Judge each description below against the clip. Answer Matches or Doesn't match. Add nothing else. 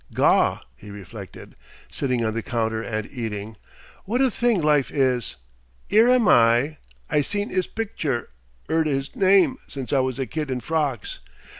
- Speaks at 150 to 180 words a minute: Matches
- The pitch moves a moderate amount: Doesn't match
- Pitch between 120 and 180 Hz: Matches